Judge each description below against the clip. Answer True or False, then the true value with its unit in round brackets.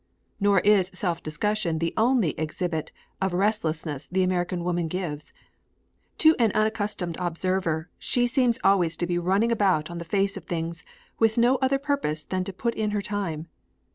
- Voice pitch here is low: False (185 Hz)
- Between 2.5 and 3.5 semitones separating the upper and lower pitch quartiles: False (4.1 semitones)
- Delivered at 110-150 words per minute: False (170 wpm)